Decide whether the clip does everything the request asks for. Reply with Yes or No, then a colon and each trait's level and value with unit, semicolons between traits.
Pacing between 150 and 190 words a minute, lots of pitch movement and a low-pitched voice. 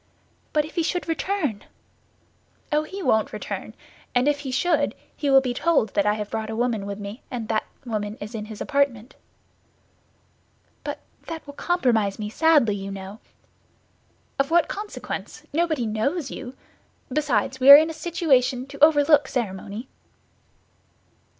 No: average, 155 wpm; wide, 5.9 semitones; very high, 265 Hz